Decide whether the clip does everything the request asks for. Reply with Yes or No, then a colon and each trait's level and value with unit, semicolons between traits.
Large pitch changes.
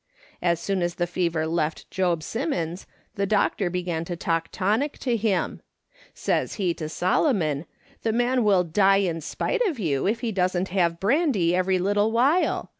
No: average, 4.1 semitones